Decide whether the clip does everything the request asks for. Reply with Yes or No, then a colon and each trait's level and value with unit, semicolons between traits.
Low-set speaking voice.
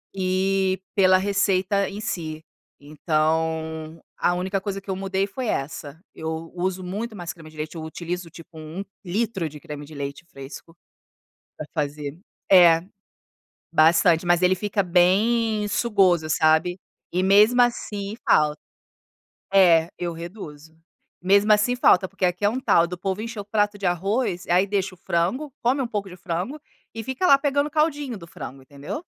No: medium, 185 Hz